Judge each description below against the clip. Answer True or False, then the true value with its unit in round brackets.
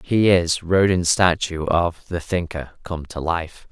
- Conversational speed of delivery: True (160 wpm)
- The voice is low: True (85 Hz)